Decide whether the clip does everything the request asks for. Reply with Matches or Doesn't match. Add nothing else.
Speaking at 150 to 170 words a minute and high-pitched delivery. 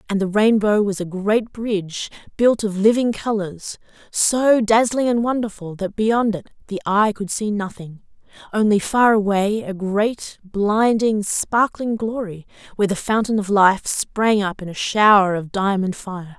Matches